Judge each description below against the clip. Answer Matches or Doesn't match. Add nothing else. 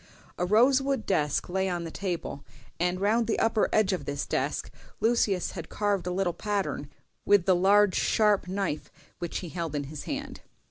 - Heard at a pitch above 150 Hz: Matches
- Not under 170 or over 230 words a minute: Matches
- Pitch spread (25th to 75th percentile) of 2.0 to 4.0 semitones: Matches